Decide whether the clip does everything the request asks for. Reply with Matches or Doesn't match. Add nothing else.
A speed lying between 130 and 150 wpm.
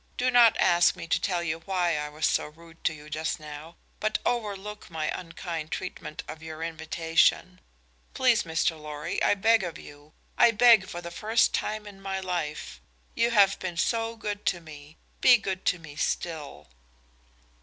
Doesn't match